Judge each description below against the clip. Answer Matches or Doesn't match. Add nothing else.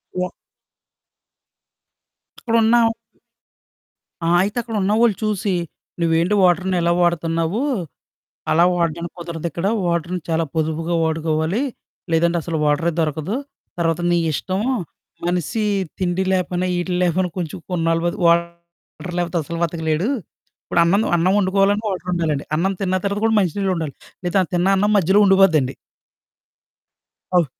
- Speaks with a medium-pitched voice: Matches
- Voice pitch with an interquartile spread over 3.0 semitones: Doesn't match